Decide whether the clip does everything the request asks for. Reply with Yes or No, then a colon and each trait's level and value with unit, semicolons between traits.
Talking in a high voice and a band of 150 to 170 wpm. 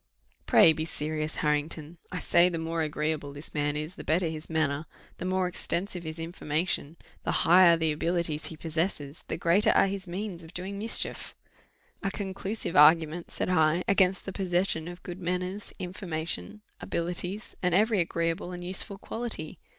No: medium, 170 Hz; average, 165 wpm